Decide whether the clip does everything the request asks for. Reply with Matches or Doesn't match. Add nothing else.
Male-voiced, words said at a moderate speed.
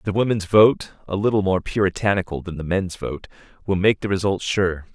Matches